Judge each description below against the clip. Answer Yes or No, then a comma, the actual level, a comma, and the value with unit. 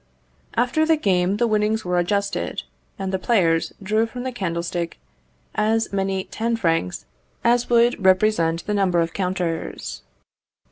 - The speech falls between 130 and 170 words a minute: Yes, average, 140 wpm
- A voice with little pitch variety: No, average, 4.2 semitones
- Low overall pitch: No, high, 195 Hz